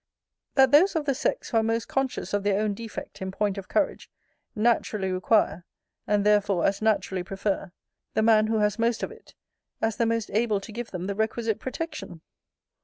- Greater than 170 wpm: Yes, average, 190 wpm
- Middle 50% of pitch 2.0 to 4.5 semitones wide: Yes, narrow, 2.6 semitones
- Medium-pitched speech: No, high, 215 Hz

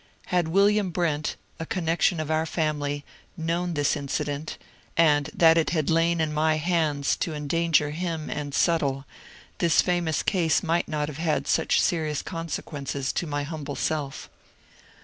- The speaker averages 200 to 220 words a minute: No, average, 150 wpm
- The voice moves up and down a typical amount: No, narrow, 2.3 semitones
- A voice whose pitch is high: No, medium, 160 Hz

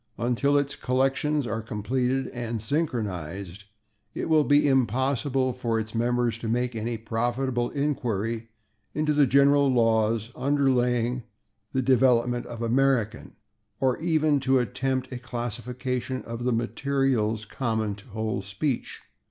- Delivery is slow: Yes, slow, 130 wpm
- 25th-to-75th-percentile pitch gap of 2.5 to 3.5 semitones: Yes, average, 2.8 semitones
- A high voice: No, low, 125 Hz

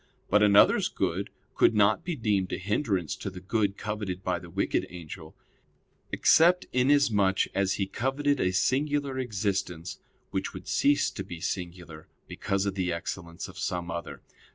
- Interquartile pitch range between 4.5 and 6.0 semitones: Yes, average, 5.3 semitones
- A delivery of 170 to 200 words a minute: No, average, 155 wpm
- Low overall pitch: Yes, low, 100 Hz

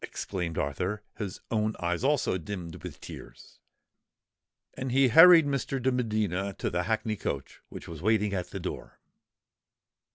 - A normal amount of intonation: No, wide, 6.0 semitones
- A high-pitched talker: No, low, 105 Hz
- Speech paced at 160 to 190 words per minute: No, average, 150 wpm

